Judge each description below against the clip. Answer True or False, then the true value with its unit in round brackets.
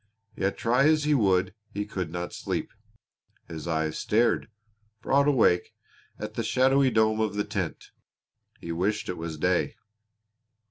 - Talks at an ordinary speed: True (145 wpm)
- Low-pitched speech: True (105 Hz)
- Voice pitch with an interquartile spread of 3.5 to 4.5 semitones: False (5.4 semitones)